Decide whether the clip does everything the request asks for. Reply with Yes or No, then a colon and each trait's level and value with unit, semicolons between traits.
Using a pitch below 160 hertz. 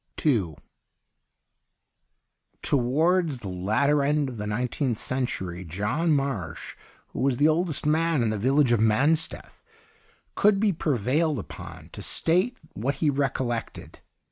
Yes: low, 135 Hz